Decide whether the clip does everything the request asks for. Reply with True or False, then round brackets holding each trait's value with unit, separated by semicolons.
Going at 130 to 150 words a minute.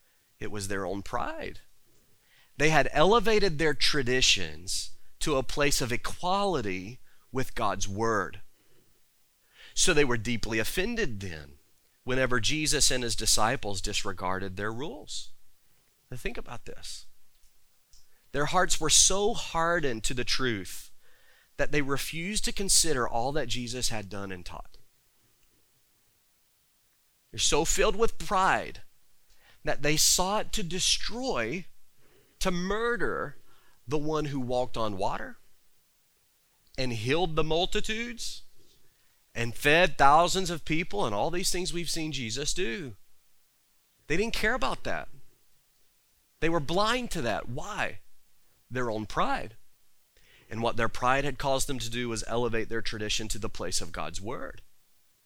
True (135 wpm)